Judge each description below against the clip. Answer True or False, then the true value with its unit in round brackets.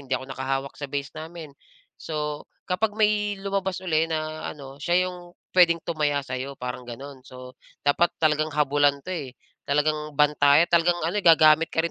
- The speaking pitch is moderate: True (155 Hz)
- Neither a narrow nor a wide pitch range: True (3.5 semitones)